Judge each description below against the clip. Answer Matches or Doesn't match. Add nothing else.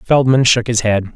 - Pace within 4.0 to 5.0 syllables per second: Matches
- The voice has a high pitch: Doesn't match